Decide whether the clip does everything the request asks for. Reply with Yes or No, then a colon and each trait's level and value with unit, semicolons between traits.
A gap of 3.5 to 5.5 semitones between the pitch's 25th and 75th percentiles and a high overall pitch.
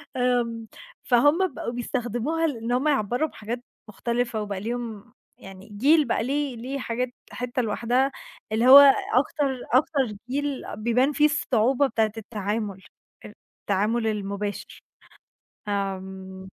Yes: average, 4.1 semitones; high, 240 Hz